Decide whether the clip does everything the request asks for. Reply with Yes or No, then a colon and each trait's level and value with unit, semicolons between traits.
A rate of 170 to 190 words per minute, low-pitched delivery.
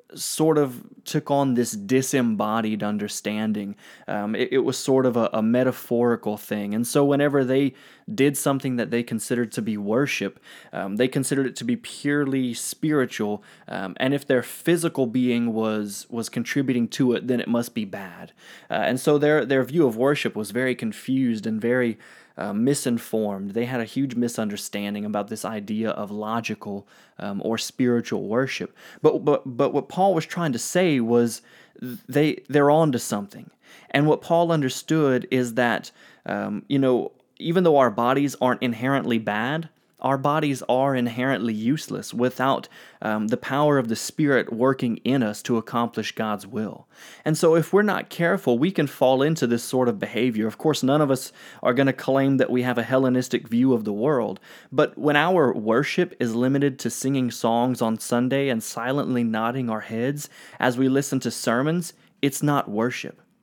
Yes: average, 180 wpm; low, 125 Hz